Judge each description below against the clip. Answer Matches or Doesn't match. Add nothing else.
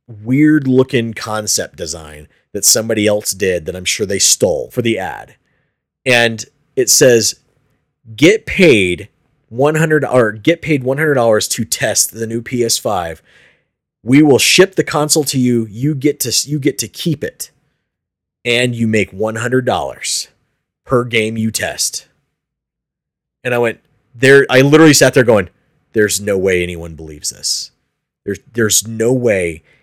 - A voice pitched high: Doesn't match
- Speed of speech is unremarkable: Matches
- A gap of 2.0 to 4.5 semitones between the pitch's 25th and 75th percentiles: Doesn't match